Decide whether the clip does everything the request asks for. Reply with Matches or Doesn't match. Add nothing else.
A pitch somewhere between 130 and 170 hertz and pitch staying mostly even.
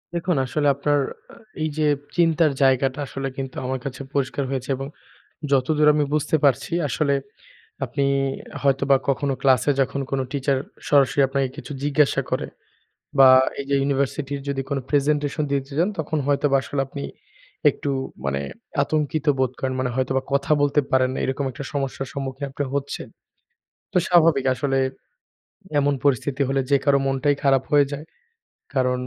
Matches